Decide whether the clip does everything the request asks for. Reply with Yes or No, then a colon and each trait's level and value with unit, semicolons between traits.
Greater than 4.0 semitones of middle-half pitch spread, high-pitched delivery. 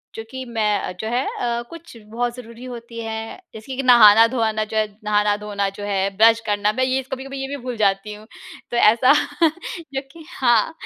No: average, 3.2 semitones; high, 230 Hz